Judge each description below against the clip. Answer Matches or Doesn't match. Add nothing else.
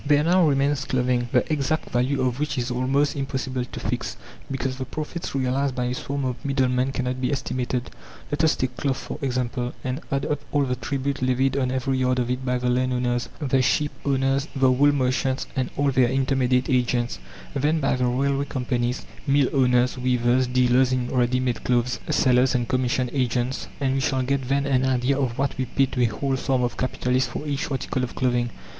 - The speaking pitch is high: Doesn't match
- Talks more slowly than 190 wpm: Doesn't match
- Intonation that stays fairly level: Matches